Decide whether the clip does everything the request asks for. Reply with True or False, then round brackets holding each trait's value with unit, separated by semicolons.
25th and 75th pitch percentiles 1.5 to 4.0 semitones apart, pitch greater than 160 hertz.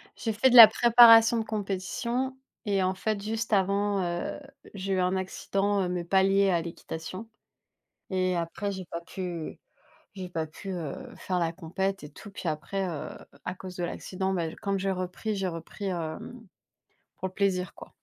True (2.4 semitones; 190 Hz)